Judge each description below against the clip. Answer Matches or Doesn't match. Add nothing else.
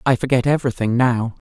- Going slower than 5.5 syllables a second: Doesn't match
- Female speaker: Doesn't match